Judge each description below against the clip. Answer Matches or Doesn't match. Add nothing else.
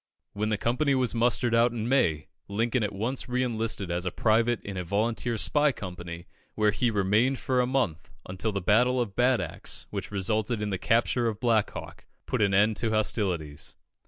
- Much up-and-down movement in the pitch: Doesn't match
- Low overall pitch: Matches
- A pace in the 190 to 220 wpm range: Matches